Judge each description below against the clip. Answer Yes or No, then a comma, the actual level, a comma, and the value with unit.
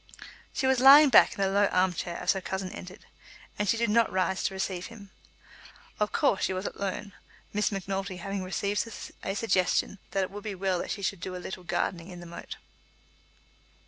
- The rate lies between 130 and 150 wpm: No, fast, 205 wpm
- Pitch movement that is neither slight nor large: No, narrow, 1.9 semitones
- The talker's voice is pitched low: No, high, 195 Hz